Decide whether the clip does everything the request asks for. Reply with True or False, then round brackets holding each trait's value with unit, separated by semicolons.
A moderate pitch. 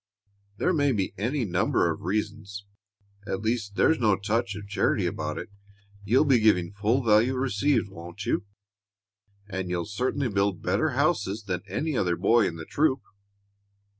False (105 Hz)